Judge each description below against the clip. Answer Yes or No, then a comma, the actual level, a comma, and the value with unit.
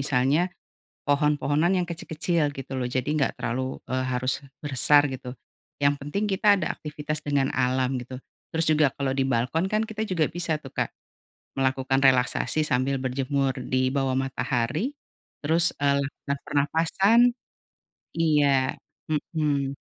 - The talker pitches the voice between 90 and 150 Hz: Yes, medium, 140 Hz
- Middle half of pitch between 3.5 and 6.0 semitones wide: No, average, 2.9 semitones